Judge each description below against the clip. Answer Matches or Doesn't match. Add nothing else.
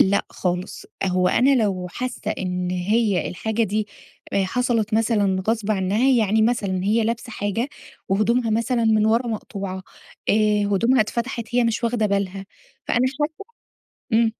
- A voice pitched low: Doesn't match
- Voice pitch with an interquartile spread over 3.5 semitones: Doesn't match